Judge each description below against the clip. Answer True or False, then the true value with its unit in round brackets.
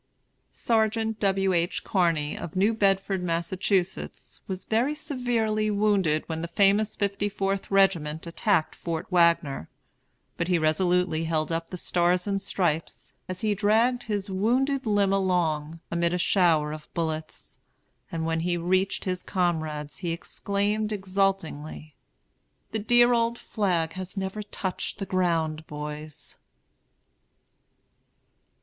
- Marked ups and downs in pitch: False (3.6 semitones)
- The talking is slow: True (130 wpm)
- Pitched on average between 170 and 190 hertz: True (185 Hz)